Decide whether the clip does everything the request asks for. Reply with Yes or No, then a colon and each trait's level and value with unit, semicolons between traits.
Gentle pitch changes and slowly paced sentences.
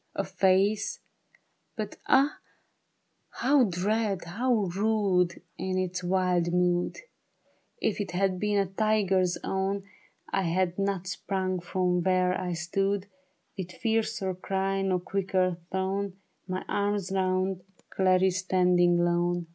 Yes: narrow, 1.7 semitones; slow, 120 wpm